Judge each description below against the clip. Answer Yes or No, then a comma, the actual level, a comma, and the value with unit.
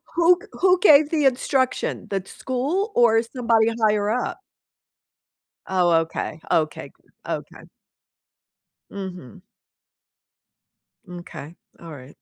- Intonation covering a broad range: Yes, wide, 8.1 semitones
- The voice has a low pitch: No, high, 225 Hz